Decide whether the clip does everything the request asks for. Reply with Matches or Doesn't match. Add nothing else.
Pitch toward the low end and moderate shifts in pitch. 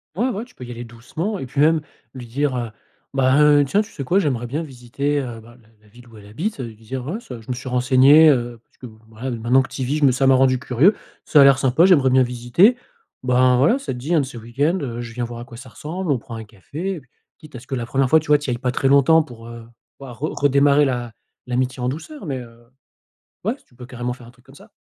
Matches